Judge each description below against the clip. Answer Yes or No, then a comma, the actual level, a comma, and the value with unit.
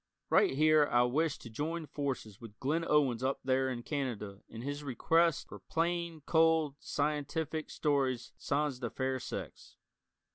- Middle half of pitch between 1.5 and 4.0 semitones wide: Yes, average, 3.6 semitones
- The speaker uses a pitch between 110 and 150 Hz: Yes, medium, 140 Hz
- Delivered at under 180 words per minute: Yes, average, 150 wpm